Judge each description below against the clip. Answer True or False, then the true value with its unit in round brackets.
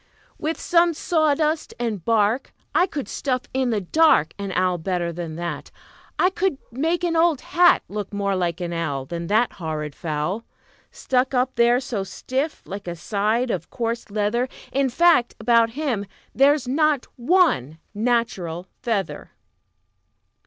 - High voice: True (230 Hz)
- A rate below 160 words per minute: True (150 wpm)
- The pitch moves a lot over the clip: True (7.1 semitones)